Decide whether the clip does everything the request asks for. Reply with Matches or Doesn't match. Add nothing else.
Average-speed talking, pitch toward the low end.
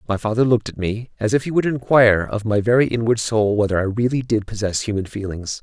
Doesn't match